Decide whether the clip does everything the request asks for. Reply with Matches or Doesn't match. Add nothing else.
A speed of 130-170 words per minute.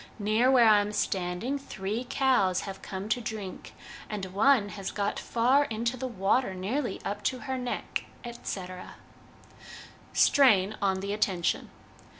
Matches